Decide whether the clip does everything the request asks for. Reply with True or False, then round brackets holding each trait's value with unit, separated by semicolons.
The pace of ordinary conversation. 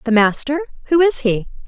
True (145 wpm)